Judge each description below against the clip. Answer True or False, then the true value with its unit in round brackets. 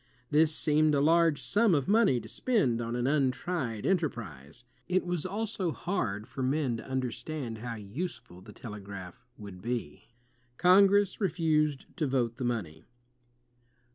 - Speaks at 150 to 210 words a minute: False (140 wpm)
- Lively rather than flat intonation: True (6.8 semitones)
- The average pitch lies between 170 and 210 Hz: False (135 Hz)